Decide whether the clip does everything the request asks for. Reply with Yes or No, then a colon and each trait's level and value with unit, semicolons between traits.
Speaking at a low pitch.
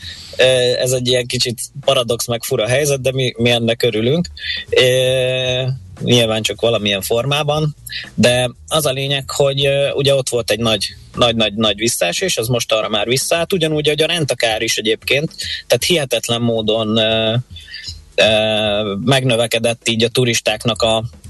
Yes: low, 120 Hz